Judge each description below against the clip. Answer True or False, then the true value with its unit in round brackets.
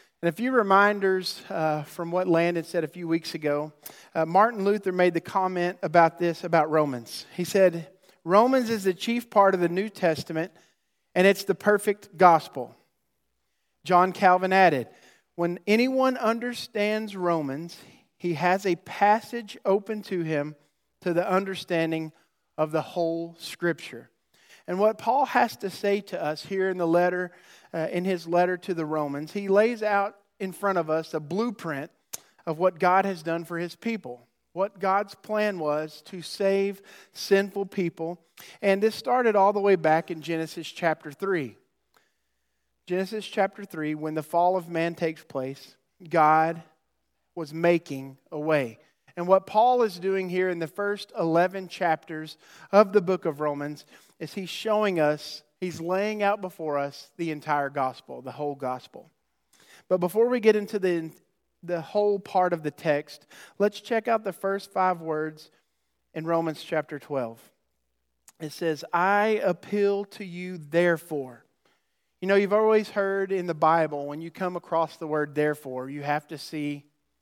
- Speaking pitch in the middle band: True (175 Hz)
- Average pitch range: True (3.9 semitones)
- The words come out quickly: False (165 wpm)